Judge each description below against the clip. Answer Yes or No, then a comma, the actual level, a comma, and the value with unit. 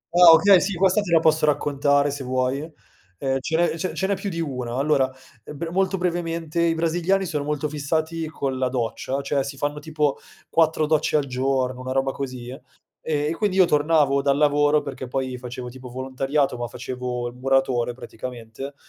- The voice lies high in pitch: No, medium, 145 Hz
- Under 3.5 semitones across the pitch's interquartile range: No, average, 3.8 semitones